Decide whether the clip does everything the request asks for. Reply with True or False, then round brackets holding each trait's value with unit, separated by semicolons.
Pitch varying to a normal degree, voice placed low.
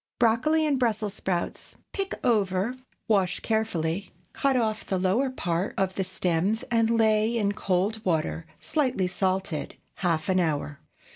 False (3.8 semitones; 200 Hz)